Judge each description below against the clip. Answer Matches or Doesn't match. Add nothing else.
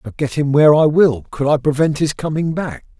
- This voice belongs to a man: Matches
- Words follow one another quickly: Matches